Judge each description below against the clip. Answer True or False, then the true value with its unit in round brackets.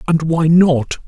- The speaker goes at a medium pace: True (170 wpm)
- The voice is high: False (160 Hz)